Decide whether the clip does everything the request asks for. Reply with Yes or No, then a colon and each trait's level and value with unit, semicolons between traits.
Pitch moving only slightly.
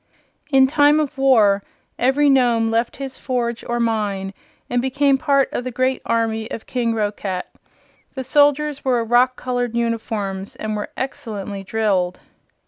No: average, 3.4 semitones